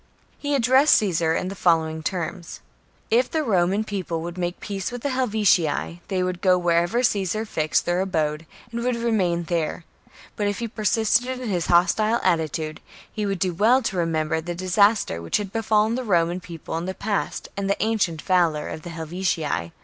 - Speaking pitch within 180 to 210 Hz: Yes, medium, 185 Hz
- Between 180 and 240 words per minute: Yes, average, 190 wpm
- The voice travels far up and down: No, average, 4.4 semitones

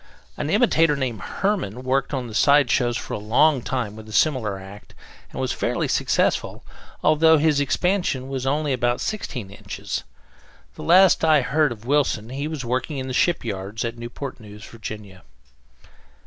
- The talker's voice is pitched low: Yes, low, 130 Hz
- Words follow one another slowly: No, average, 165 wpm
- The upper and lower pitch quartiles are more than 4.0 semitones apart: Yes, average, 5.1 semitones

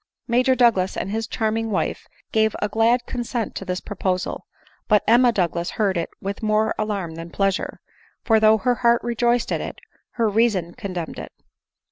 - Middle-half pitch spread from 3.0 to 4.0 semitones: Yes, average, 3.5 semitones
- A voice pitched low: No, high, 215 Hz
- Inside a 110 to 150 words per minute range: No, average, 170 wpm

